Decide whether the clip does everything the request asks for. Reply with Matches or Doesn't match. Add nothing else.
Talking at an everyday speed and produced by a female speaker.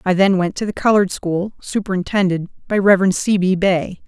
Matches